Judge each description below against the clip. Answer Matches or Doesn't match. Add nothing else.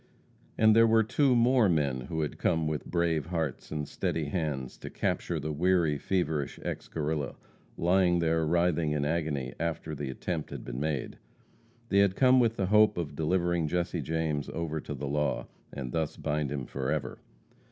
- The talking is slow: Doesn't match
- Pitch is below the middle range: Matches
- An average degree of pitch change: Matches